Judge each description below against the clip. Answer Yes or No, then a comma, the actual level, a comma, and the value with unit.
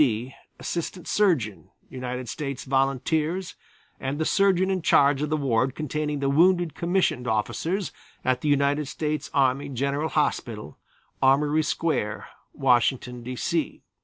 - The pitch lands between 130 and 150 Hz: Yes, medium, 140 Hz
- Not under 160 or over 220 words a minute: No, slow, 135 wpm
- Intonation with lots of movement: No, average, 3.7 semitones